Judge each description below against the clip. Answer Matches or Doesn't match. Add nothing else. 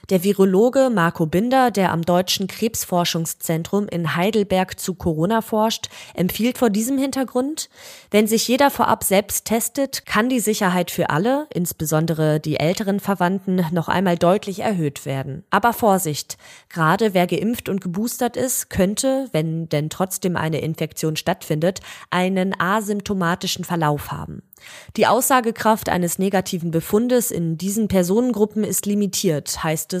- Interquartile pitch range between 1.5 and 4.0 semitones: Doesn't match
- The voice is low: Doesn't match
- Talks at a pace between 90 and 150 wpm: Matches